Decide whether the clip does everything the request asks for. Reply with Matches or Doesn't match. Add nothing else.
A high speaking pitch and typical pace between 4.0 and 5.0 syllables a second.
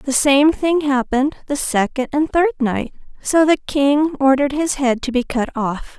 Matches